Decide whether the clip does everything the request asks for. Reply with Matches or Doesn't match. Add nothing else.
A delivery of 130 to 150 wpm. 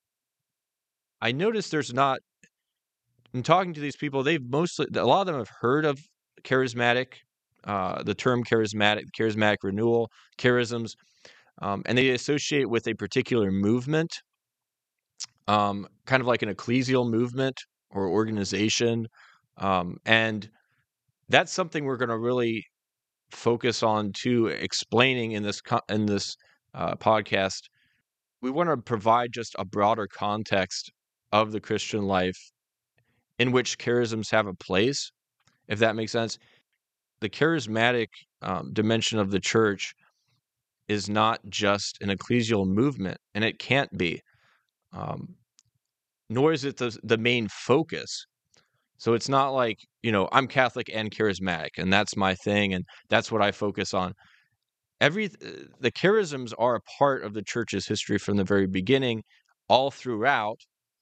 Matches